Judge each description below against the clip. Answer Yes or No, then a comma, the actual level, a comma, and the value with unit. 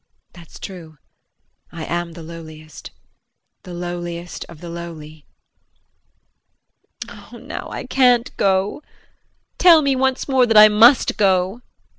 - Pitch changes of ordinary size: No, wide, 5.7 semitones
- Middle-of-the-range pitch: Yes, medium, 180 Hz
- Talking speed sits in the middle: No, slow, 125 wpm